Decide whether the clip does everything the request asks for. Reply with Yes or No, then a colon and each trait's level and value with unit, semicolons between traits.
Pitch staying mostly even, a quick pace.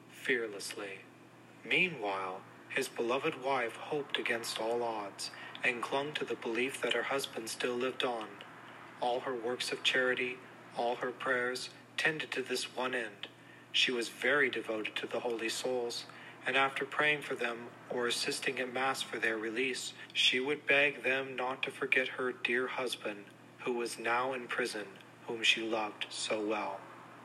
No: narrow, 1.8 semitones; average, 160 wpm